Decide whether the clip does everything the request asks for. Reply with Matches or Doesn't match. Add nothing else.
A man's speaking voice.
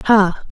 Doesn't match